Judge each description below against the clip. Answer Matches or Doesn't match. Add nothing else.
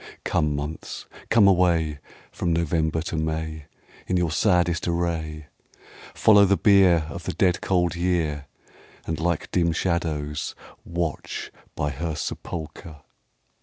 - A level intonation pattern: Matches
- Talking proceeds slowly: Matches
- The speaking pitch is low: Matches